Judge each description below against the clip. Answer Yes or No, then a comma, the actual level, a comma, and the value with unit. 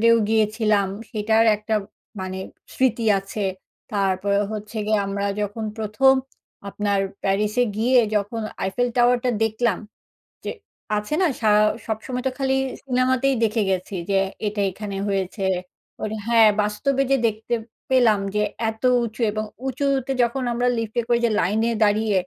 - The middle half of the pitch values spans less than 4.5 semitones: Yes, average, 2.8 semitones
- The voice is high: Yes, high, 220 Hz